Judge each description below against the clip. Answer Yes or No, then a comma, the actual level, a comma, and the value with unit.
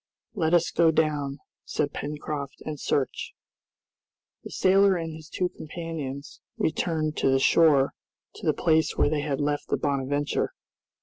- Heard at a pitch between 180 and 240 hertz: No, medium, 155 Hz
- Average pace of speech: Yes, average, 145 wpm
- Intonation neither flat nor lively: No, narrow, 2.3 semitones